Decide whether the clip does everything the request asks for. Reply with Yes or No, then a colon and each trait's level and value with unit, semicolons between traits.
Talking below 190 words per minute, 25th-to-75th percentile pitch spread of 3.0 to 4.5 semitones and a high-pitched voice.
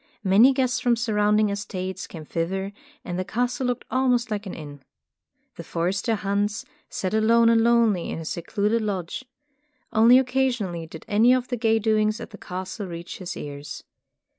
Yes: average, 170 wpm; average, 4.0 semitones; high, 210 Hz